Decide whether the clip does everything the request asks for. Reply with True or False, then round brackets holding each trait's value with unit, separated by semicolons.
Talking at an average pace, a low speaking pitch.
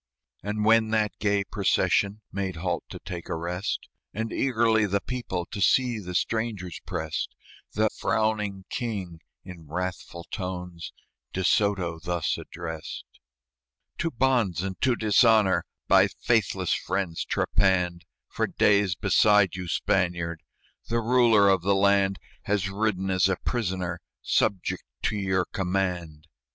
False (130 wpm; 95 Hz)